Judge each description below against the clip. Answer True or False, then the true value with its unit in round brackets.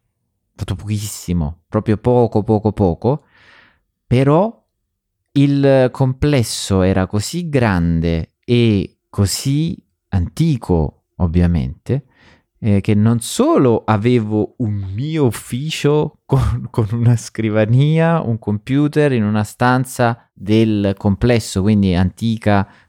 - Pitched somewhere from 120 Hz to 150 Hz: False (110 Hz)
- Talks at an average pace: False (95 wpm)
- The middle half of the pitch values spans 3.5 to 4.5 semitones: True (4.1 semitones)